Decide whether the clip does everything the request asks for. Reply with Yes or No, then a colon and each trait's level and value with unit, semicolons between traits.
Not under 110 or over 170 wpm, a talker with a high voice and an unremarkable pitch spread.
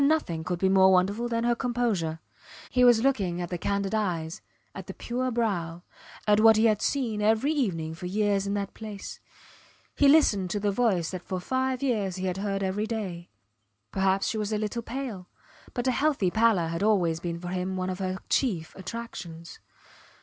No: average, 195 wpm; high, 200 Hz; average, 4.1 semitones